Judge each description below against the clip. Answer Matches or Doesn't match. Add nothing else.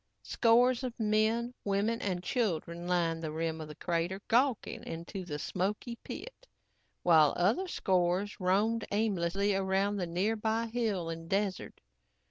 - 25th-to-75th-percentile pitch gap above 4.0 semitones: Matches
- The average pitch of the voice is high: Matches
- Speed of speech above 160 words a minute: Doesn't match